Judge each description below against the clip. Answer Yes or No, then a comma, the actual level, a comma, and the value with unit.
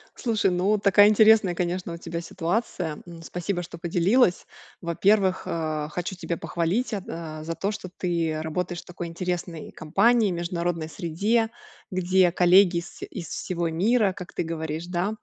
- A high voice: No, medium, 175 Hz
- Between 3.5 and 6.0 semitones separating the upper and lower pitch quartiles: No, average, 2.7 semitones